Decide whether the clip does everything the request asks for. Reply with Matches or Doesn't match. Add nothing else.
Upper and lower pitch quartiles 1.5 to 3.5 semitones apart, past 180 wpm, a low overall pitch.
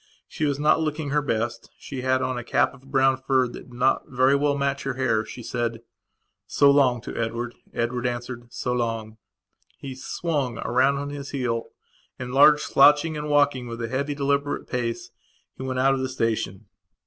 Matches